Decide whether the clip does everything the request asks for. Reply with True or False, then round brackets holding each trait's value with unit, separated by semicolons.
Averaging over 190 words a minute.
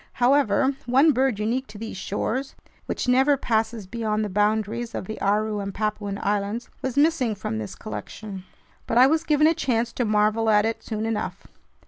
False (180 wpm)